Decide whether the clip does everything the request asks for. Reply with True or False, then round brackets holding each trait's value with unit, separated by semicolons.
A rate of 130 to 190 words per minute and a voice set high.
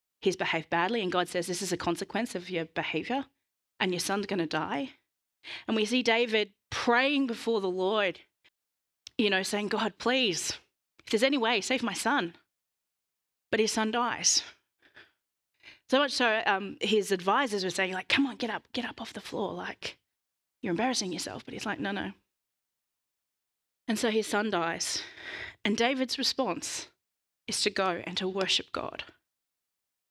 True (170 wpm; 215 Hz)